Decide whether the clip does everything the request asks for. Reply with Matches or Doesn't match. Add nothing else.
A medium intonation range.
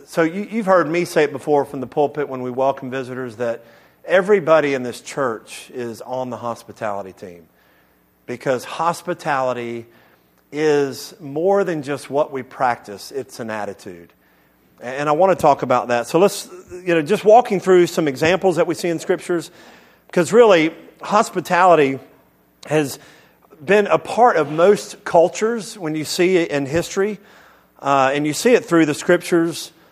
Doesn't match